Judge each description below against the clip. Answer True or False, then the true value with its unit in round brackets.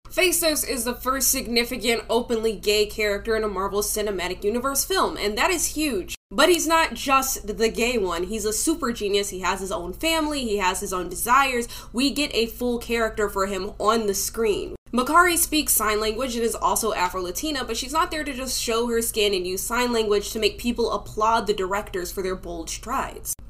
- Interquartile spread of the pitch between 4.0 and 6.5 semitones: True (4.6 semitones)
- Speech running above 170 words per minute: True (205 wpm)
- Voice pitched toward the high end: True (225 Hz)